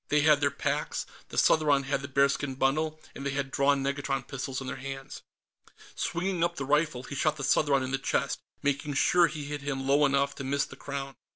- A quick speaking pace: Yes, fast, 215 wpm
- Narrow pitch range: Yes, narrow, 1.6 semitones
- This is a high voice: No, medium, 140 Hz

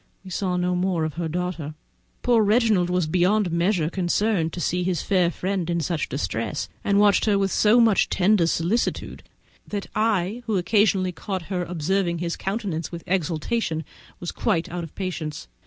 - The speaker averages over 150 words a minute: Yes, average, 170 wpm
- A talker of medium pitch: Yes, medium, 180 Hz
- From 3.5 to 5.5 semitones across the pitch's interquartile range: No, average, 2.9 semitones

